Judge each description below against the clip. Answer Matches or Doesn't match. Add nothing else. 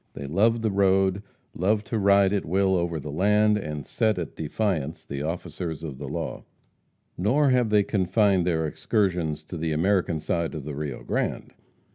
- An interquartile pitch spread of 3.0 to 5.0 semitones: Matches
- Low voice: Matches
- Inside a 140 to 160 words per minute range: Doesn't match